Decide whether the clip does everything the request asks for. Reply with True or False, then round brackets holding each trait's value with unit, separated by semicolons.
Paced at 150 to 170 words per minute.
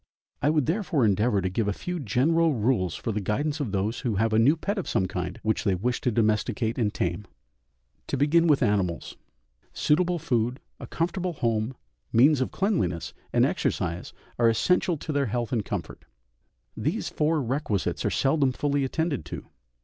False (180 wpm)